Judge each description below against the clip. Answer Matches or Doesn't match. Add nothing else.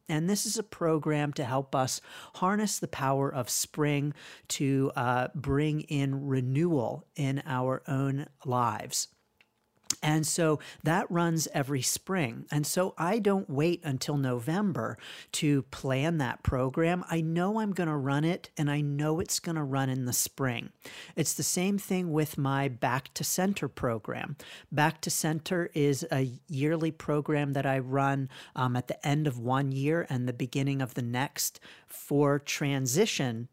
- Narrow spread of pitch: Doesn't match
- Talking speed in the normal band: Matches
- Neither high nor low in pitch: Matches